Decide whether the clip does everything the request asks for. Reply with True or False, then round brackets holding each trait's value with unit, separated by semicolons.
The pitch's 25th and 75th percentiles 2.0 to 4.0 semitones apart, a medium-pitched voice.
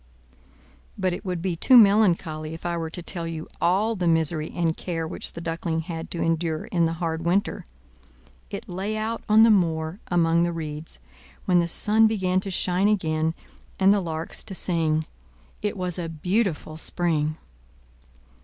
True (2.8 semitones; 170 Hz)